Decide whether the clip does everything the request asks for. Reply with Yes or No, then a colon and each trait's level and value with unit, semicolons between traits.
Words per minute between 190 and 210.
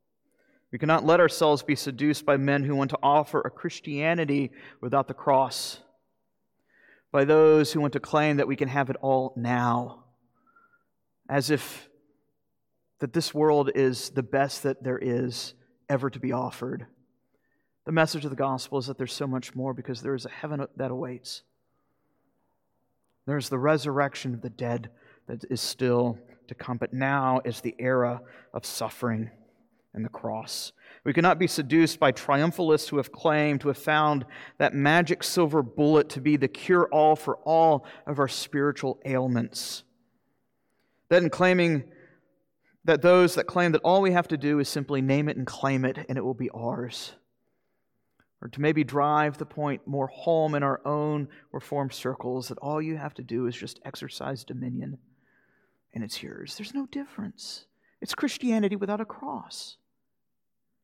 No: average, 170 wpm